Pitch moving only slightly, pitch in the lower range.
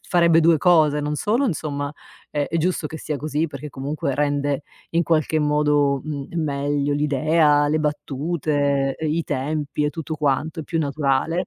No: narrow, 1.9 semitones; medium, 150 Hz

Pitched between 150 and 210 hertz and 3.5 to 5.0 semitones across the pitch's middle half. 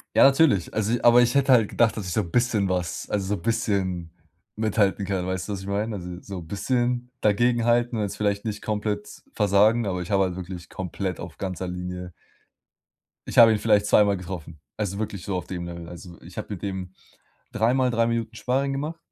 No: low, 100 Hz; average, 3.9 semitones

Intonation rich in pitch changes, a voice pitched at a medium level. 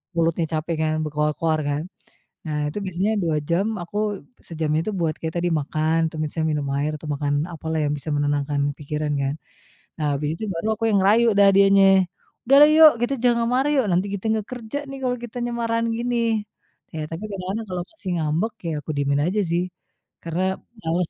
Yes: wide, 5.9 semitones; medium, 170 Hz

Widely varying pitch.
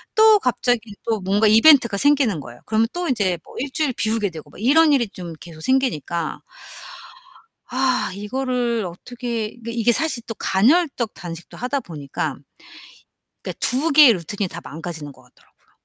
Yes: wide, 6.2 semitones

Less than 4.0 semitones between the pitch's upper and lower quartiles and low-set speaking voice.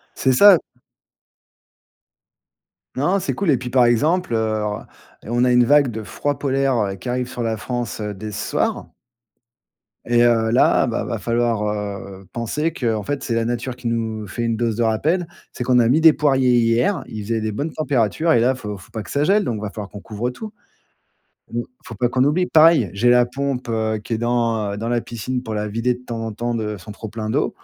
Yes: average, 2.9 semitones; low, 120 Hz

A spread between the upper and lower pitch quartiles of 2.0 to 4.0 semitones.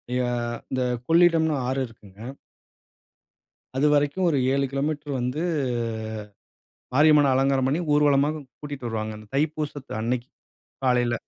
Yes: average, 2.8 semitones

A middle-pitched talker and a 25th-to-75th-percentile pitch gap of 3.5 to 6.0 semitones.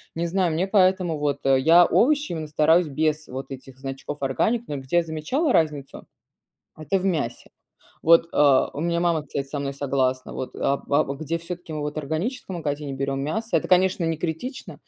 Yes: medium, 155 Hz; average, 3.8 semitones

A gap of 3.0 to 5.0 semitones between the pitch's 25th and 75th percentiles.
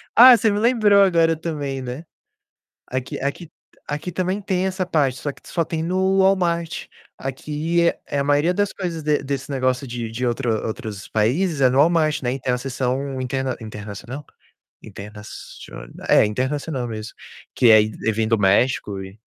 No: wide, 5.6 semitones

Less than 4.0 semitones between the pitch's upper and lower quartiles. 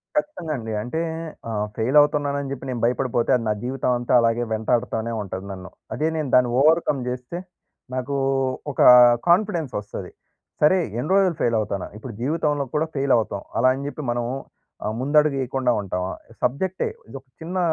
No: average, 4.5 semitones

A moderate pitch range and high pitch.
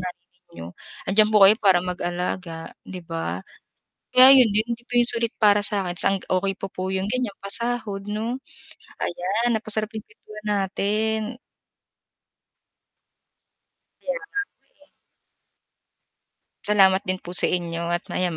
Yes: average, 3.2 semitones; high, 200 Hz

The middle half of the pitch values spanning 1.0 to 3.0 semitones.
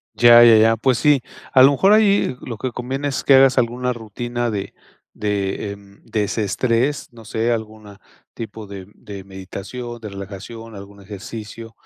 No: average, 3.4 semitones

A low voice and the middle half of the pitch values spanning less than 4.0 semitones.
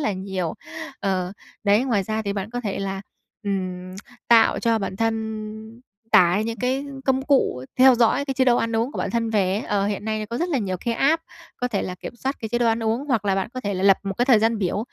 No: high, 220 Hz; average, 3.5 semitones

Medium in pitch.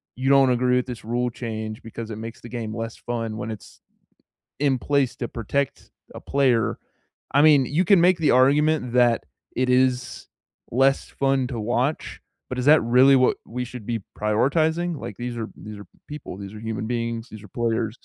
No: low, 125 Hz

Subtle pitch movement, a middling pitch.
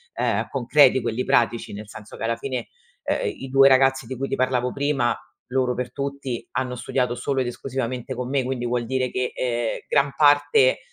No: narrow, 2.0 semitones; low, 130 Hz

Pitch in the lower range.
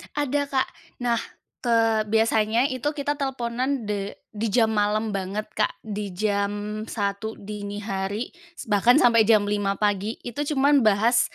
No: high, 220 Hz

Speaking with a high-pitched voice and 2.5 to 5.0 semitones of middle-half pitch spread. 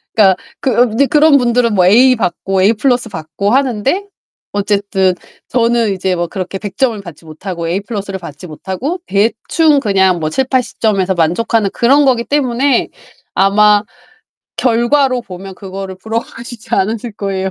Yes: high, 210 Hz; average, 4.4 semitones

